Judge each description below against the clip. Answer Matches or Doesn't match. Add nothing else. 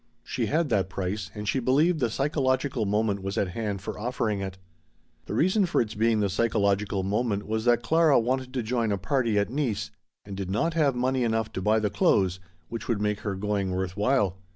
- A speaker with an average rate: Doesn't match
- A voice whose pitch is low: Matches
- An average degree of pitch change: Matches